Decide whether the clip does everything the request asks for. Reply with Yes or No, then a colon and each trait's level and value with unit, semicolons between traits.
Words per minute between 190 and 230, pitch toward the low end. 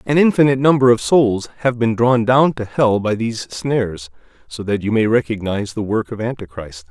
Yes: average, 200 wpm; low, 115 Hz